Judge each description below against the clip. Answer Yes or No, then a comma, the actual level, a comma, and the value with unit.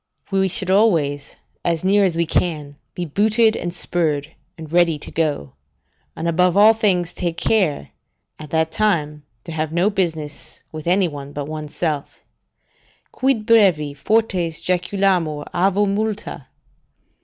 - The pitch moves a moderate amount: Yes, average, 4.3 semitones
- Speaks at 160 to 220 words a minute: No, average, 145 wpm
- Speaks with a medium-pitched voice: Yes, medium, 175 Hz